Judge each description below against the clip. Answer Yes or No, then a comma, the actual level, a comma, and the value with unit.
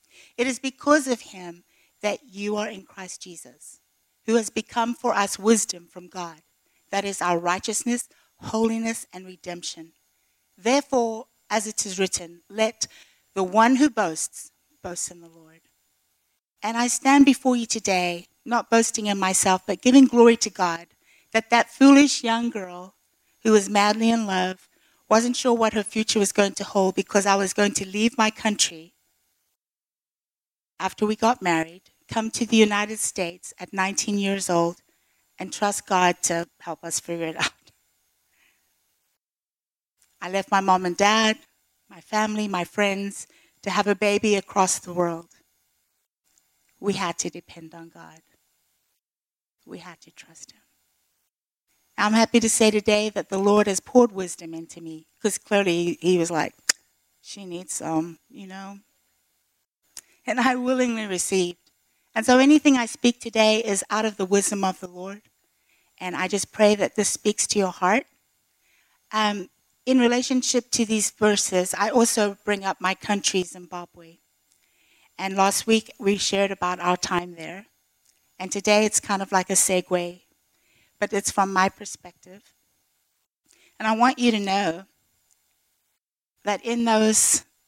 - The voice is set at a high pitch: Yes, high, 195 Hz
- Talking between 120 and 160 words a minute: Yes, average, 155 wpm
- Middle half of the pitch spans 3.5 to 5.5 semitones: Yes, average, 4.1 semitones